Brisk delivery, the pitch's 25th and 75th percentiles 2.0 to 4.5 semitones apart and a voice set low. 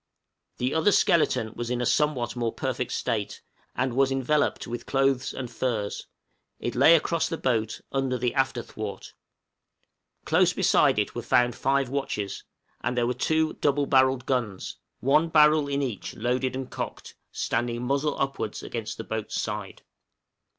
No: average, 155 wpm; average, 2.8 semitones; low, 130 Hz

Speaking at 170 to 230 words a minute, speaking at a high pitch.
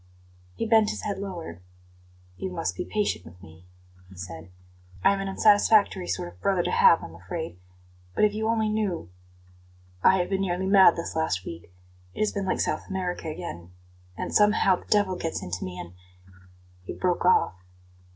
No: average, 185 wpm; medium, 180 Hz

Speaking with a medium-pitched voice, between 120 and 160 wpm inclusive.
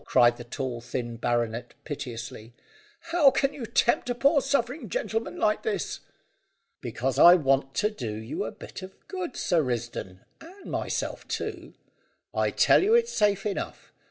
Yes: medium, 175 Hz; average, 155 wpm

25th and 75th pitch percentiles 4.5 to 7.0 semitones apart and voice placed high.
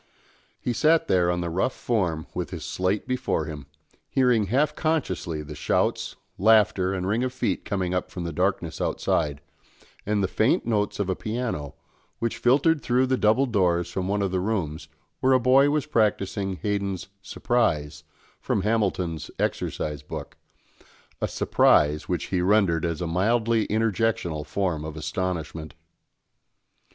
No: average, 5.1 semitones; very low, 95 Hz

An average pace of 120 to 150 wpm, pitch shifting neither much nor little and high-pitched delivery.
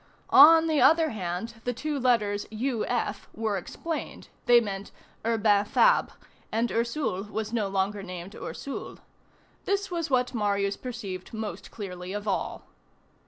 Yes: average, 140 wpm; average, 4.1 semitones; high, 220 Hz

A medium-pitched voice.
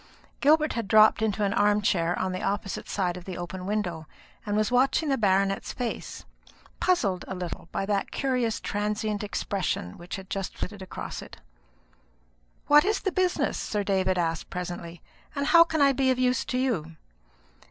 No: high, 205 Hz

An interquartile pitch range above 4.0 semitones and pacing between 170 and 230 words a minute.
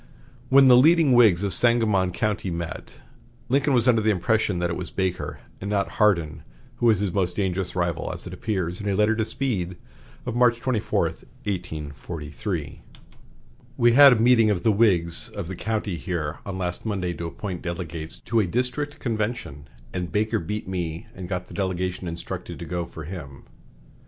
Yes: average, 4.4 semitones; average, 175 wpm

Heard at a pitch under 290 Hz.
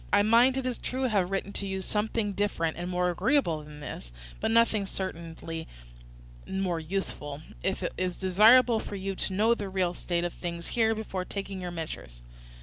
Yes: high, 190 Hz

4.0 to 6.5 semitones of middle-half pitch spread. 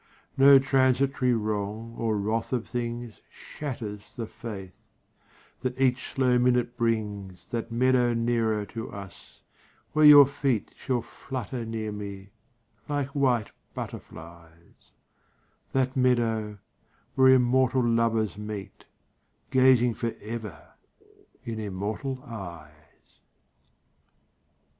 No: average, 3.4 semitones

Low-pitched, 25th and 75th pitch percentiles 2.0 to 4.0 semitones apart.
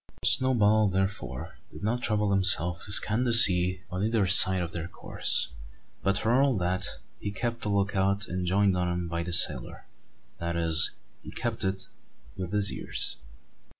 Yes: very low, 95 Hz; average, 2.9 semitones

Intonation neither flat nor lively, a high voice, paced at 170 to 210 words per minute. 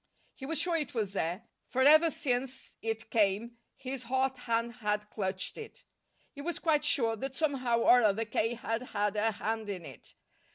Yes: average, 3.9 semitones; high, 235 Hz; average, 180 wpm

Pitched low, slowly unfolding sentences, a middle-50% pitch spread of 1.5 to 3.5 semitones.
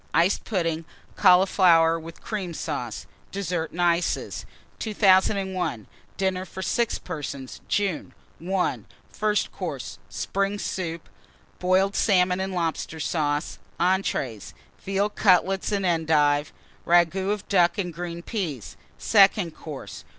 No: medium, 180 Hz; slow, 115 wpm; average, 2.9 semitones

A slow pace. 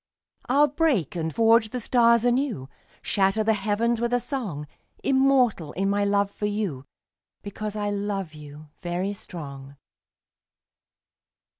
Yes: slow, 130 wpm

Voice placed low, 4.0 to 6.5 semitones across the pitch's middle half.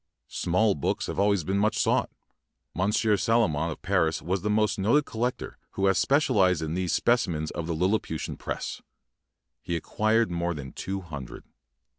Yes: very low, 95 Hz; average, 4.3 semitones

